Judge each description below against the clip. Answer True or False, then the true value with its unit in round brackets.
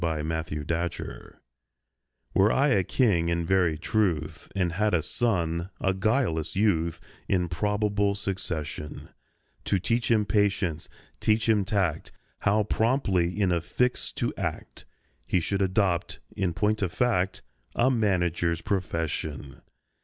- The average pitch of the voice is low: True (95 Hz)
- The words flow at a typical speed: False (130 wpm)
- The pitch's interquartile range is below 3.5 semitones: False (3.8 semitones)